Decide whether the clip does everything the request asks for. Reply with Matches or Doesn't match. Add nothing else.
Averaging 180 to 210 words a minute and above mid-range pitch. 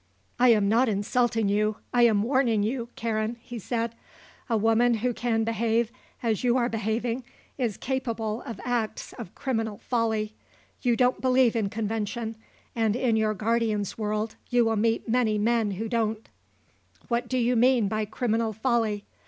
Doesn't match